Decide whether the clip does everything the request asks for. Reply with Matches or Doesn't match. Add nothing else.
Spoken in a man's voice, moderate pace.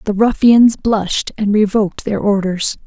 Doesn't match